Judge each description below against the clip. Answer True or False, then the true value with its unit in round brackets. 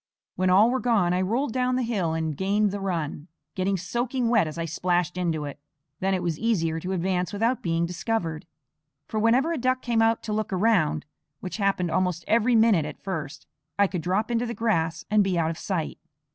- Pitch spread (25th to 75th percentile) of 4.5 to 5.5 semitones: True (5.1 semitones)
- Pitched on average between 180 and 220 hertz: True (190 Hz)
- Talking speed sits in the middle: False (210 wpm)